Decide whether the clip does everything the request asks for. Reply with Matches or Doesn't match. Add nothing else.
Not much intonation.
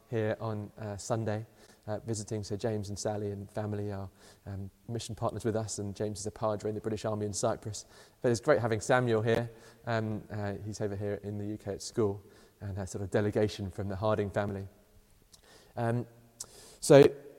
Matches